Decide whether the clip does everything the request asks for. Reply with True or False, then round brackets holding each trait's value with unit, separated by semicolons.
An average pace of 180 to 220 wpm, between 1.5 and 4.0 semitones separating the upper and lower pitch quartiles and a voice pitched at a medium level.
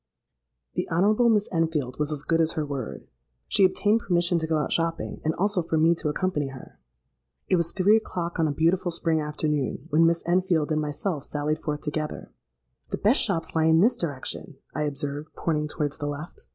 True (195 wpm; 2.8 semitones; 160 Hz)